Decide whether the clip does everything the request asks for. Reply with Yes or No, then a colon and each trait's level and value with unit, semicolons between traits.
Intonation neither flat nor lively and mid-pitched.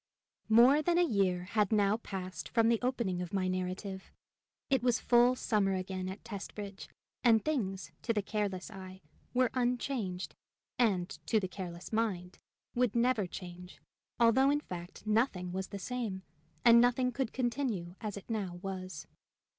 No: average, 4.4 semitones; high, 210 Hz